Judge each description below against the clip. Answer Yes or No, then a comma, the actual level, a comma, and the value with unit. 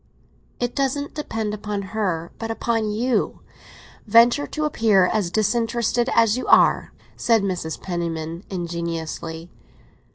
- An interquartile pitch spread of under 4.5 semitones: No, average, 5.3 semitones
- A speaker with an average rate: No, slow, 120 wpm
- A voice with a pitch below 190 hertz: No, high, 210 Hz